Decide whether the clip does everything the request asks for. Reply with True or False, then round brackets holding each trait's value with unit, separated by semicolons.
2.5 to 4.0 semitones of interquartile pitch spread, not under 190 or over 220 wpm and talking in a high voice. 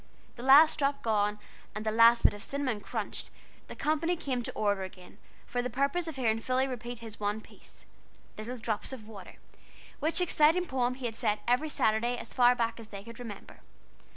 True (3.7 semitones; 195 wpm; 240 Hz)